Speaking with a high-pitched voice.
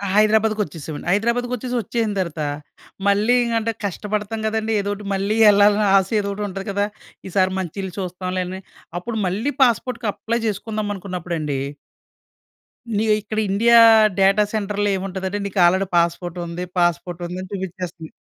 Yes: high, 200 Hz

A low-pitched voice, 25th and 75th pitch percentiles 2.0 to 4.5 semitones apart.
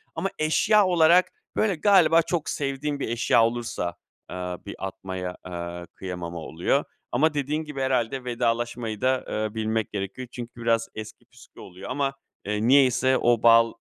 No: low, 120 Hz; average, 5.3 semitones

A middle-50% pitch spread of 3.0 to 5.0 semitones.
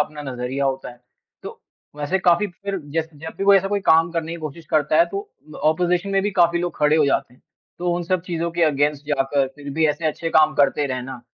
Yes: average, 3.3 semitones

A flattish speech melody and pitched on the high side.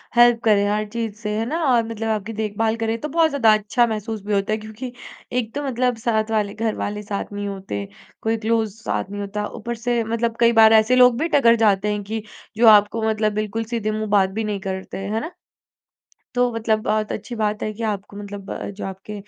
Yes: narrow, 1.9 semitones; high, 220 Hz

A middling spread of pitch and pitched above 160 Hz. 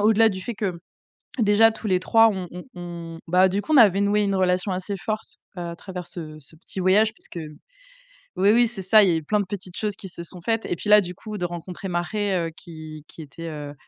Yes: average, 3.3 semitones; medium, 185 Hz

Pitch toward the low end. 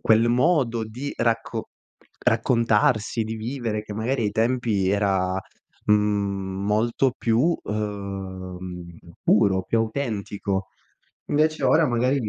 Yes: low, 110 Hz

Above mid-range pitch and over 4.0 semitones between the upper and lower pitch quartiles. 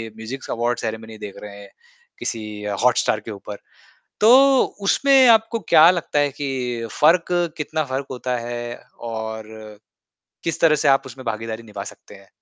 No: low, 120 Hz; average, 5.3 semitones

